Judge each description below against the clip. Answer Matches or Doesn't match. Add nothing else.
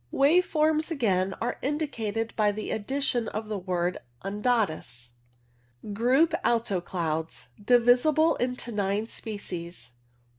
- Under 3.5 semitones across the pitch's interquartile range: Doesn't match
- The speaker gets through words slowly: Matches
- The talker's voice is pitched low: Doesn't match